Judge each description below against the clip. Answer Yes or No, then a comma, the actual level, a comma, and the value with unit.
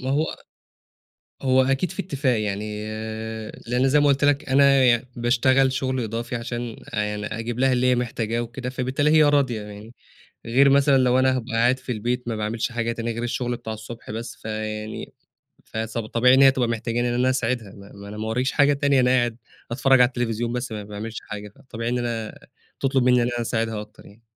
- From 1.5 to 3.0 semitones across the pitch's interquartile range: Yes, narrow, 2.6 semitones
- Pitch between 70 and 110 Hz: No, low, 120 Hz